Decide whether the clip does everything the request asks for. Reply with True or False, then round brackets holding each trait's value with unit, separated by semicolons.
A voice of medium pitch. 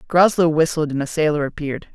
True (155 Hz)